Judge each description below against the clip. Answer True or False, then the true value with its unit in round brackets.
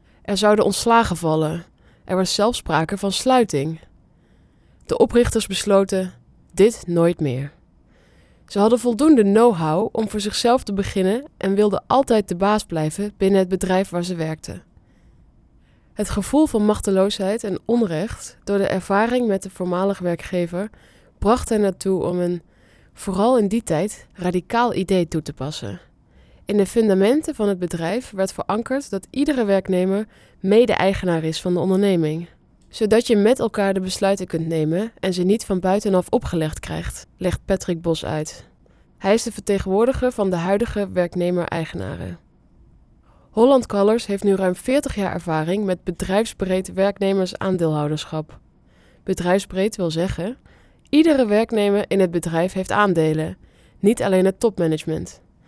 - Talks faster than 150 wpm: False (145 wpm)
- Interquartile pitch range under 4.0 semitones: True (3.2 semitones)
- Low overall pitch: False (195 Hz)